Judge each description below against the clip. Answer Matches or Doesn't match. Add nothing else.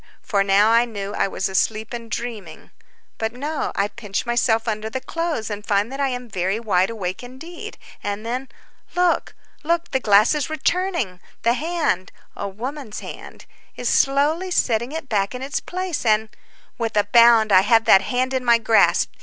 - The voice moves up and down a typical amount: Matches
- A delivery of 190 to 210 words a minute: Doesn't match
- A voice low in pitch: Doesn't match